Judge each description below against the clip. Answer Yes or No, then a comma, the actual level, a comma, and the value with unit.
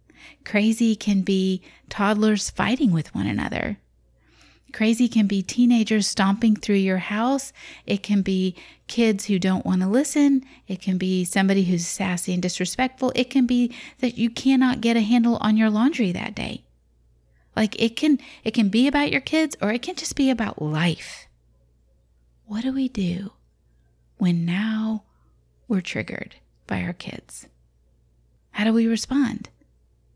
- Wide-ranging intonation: Yes, wide, 5.7 semitones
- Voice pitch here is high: Yes, high, 205 Hz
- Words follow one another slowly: No, average, 155 wpm